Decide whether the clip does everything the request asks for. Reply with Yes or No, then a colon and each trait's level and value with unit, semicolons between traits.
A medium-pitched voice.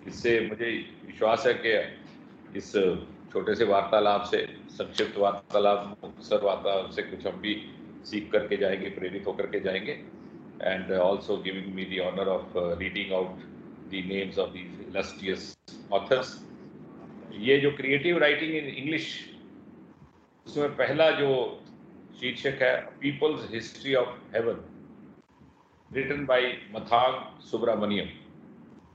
No: low, 110 Hz